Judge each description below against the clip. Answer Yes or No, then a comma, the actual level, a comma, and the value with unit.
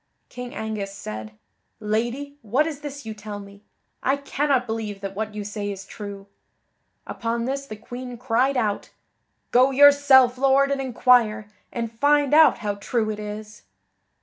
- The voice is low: No, high, 230 Hz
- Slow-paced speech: No, average, 155 wpm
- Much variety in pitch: No, average, 4.4 semitones